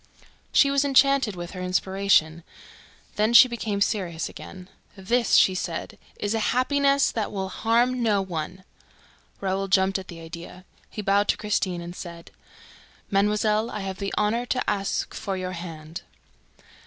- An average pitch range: Yes, average, 3.5 semitones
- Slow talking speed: No, average, 155 wpm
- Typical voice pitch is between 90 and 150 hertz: No, high, 195 Hz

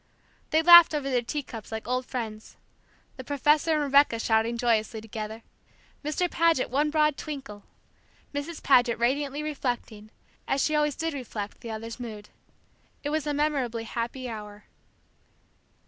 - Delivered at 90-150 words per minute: Yes, average, 145 wpm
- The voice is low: No, very high, 255 Hz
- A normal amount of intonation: Yes, average, 4.7 semitones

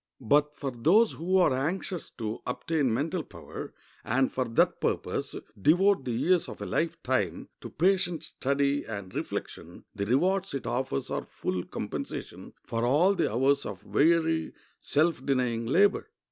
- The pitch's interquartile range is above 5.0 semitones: Yes, wide, 5.6 semitones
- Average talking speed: Yes, average, 155 wpm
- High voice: No, medium, 140 Hz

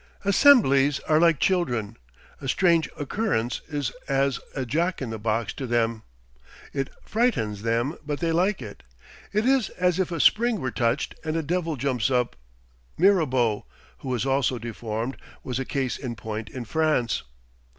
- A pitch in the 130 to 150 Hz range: Yes, low, 135 Hz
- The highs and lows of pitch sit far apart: Yes, wide, 6.2 semitones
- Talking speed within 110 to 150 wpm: No, average, 160 wpm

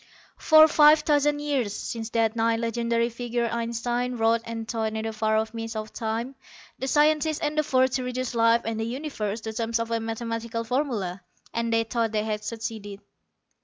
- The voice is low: No, high, 230 Hz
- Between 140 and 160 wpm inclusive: No, average, 190 wpm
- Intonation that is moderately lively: No, narrow, 2.1 semitones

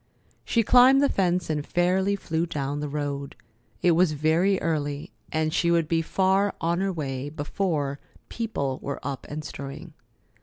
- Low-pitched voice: No, medium, 160 Hz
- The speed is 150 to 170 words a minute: Yes, average, 160 wpm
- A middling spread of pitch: Yes, average, 4.2 semitones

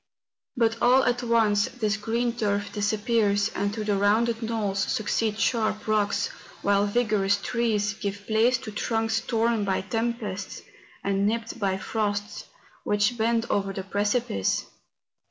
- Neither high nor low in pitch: No, high, 215 Hz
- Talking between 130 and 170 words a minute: Yes, slow, 135 wpm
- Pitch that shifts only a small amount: Yes, narrow, 2.2 semitones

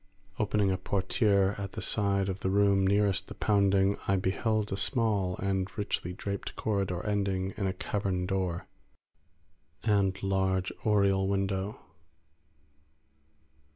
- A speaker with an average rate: No, slow, 125 wpm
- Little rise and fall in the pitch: Yes, narrow, 1.2 semitones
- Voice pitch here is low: Yes, low, 100 Hz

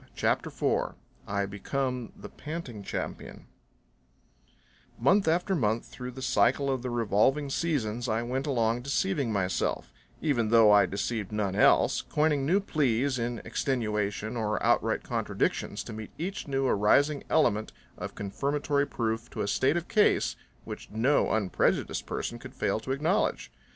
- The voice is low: Yes, low, 120 Hz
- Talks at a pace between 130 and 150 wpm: Yes, average, 145 wpm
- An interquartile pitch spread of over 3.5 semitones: Yes, average, 4.7 semitones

